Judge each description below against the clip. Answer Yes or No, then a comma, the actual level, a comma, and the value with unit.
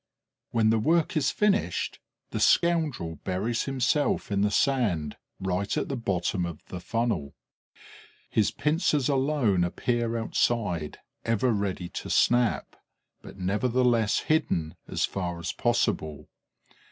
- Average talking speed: No, slow, 125 wpm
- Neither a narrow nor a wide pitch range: No, wide, 6.2 semitones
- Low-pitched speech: Yes, low, 115 Hz